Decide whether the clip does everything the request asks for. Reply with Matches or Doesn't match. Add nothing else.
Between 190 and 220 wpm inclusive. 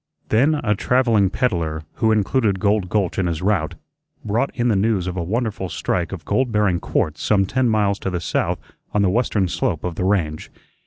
Matches